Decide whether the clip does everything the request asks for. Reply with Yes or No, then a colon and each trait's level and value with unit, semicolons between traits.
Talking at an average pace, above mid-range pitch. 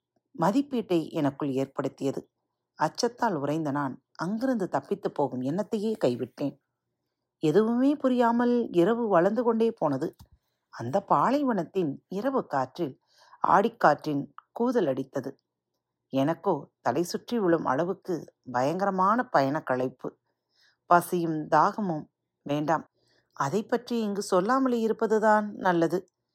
No: average, 90 wpm; medium, 180 Hz